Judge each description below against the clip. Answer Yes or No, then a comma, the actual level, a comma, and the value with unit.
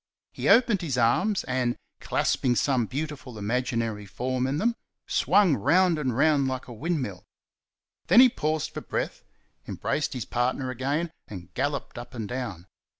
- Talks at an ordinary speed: Yes, average, 150 wpm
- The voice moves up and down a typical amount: Yes, average, 4.5 semitones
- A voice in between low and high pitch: No, low, 130 Hz